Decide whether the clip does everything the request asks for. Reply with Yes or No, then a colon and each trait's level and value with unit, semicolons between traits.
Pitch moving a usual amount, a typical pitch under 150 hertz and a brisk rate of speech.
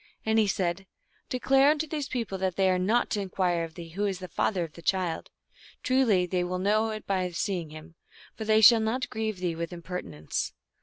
No: average, 3.9 semitones; high, 190 Hz; fast, 240 wpm